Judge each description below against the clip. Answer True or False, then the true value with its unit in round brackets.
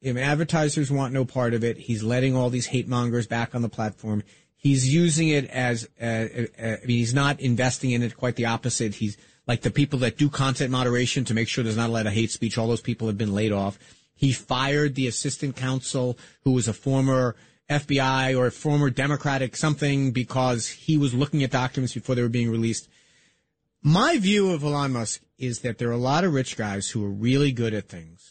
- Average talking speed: False (220 wpm)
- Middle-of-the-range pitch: False (125 Hz)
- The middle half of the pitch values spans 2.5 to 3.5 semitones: True (3.1 semitones)